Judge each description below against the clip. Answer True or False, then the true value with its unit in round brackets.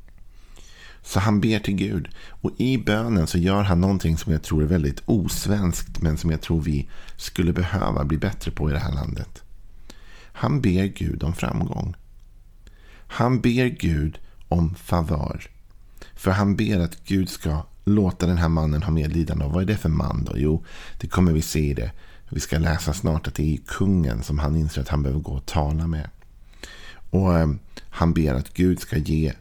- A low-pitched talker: True (85 Hz)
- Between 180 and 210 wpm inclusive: True (190 wpm)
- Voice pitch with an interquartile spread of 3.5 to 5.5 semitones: True (3.9 semitones)